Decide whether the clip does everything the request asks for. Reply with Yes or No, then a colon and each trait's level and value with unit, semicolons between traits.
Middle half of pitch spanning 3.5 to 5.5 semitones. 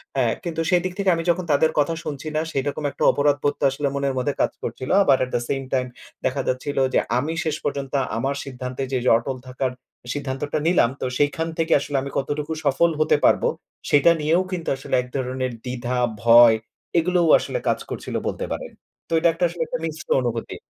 Yes: average, 3.8 semitones